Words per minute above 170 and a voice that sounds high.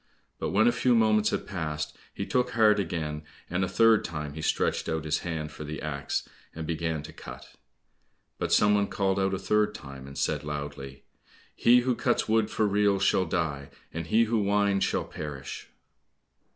No: average, 190 wpm; very low, 90 Hz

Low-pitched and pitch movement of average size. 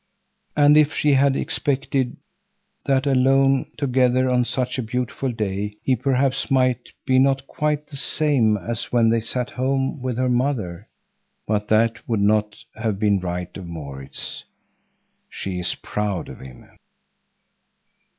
Yes: low, 125 Hz; average, 4.3 semitones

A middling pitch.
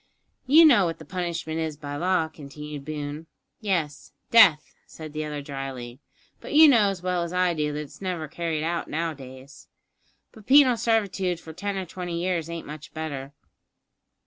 Yes: medium, 165 Hz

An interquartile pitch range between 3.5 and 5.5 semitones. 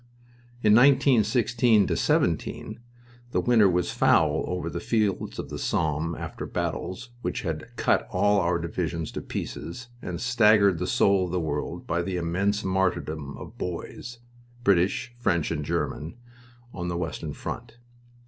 Yes: average, 4.5 semitones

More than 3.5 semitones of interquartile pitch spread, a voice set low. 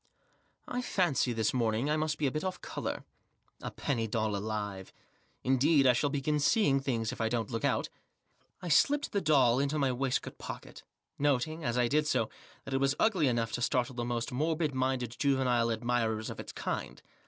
Yes: average, 4.2 semitones; low, 130 Hz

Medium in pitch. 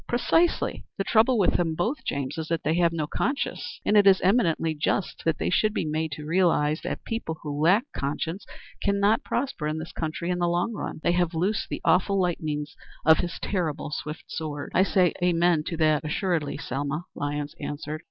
Yes: medium, 165 Hz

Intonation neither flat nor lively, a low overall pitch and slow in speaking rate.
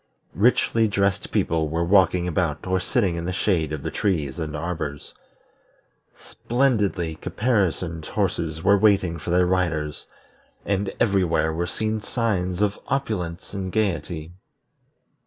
Yes: average, 3.6 semitones; very low, 90 Hz; slow, 130 wpm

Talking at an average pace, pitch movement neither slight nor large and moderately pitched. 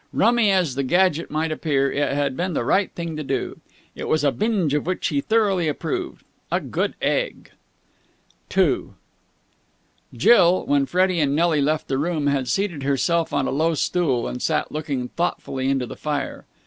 Yes: average, 175 wpm; average, 4.4 semitones; medium, 155 Hz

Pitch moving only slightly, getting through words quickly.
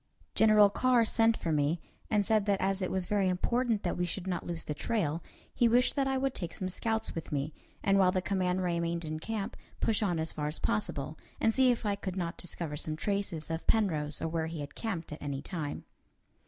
No: average, 4.9 semitones; fast, 225 wpm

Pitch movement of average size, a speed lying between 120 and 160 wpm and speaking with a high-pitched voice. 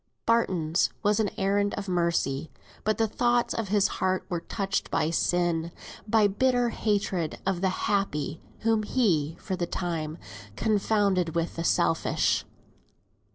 Yes: average, 3.8 semitones; average, 140 wpm; high, 195 Hz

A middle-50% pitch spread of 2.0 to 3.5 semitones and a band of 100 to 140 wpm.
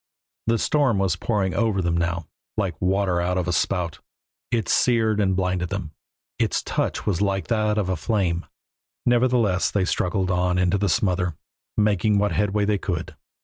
No: average, 2.8 semitones; average, 170 wpm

